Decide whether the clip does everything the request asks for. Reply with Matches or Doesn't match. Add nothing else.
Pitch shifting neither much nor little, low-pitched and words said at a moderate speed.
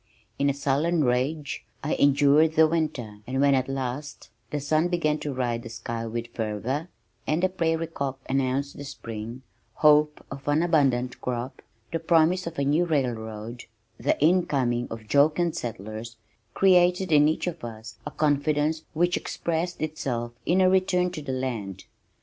Doesn't match